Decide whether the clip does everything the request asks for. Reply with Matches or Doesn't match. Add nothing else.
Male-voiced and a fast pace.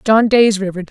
Doesn't match